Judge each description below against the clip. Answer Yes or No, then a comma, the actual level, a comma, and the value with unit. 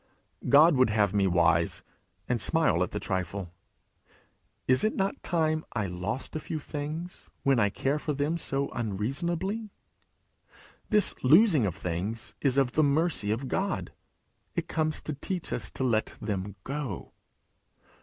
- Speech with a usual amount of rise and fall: No, wide, 7.3 semitones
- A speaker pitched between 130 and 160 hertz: Yes, low, 135 Hz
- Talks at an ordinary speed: Yes, average, 150 wpm